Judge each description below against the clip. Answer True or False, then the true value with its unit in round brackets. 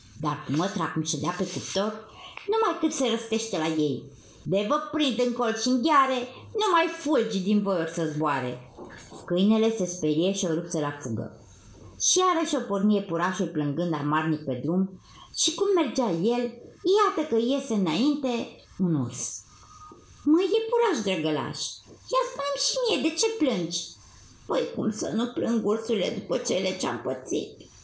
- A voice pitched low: False (205 Hz)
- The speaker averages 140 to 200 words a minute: True (165 wpm)